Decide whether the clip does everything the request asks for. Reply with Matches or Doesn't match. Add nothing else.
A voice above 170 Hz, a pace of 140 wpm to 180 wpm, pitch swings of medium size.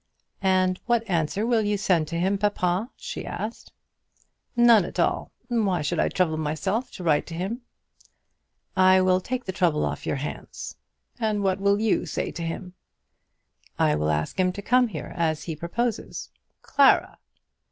Matches